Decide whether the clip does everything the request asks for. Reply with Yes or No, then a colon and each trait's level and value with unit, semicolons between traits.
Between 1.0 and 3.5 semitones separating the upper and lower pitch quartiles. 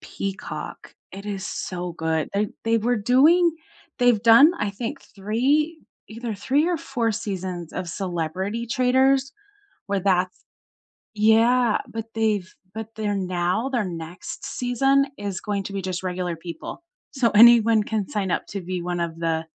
No: average, 4.7 semitones